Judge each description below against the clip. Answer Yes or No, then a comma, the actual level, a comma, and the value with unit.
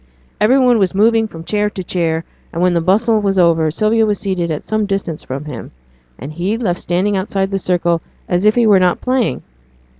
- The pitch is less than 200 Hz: Yes, high, 190 Hz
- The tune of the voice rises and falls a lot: No, average, 3.8 semitones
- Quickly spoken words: Yes, fast, 210 wpm